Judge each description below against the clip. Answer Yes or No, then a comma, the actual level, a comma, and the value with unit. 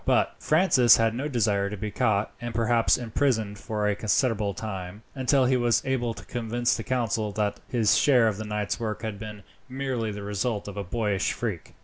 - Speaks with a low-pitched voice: Yes, low, 110 Hz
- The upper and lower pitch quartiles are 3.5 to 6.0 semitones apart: No, average, 2.8 semitones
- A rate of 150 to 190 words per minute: No, average, 200 wpm